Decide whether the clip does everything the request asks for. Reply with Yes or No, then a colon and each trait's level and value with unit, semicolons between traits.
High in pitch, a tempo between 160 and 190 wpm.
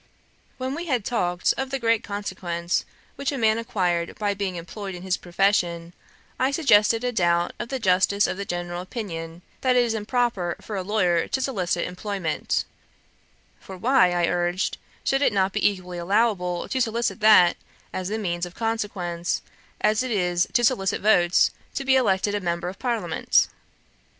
Yes: high, 200 Hz; average, 175 wpm